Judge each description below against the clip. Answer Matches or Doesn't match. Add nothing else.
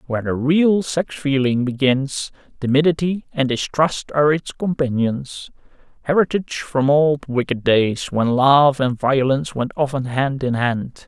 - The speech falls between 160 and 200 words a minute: Doesn't match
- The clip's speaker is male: Matches